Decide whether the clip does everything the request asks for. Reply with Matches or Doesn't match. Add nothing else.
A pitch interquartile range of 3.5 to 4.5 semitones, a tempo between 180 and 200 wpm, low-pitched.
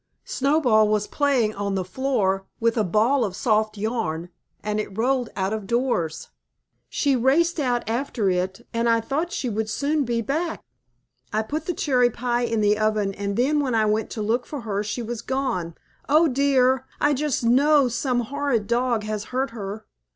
Doesn't match